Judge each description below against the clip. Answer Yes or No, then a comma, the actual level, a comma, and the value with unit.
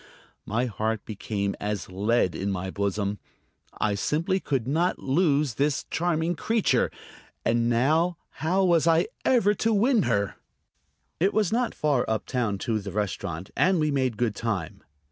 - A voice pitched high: No, low, 130 Hz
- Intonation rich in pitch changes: Yes, wide, 8.5 semitones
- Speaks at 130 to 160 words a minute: Yes, average, 155 wpm